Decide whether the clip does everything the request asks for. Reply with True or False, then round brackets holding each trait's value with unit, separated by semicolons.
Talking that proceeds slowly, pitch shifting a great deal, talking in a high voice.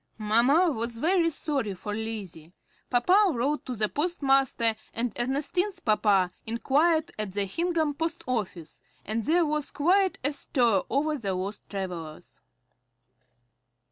True (130 wpm; 6.7 semitones; 250 Hz)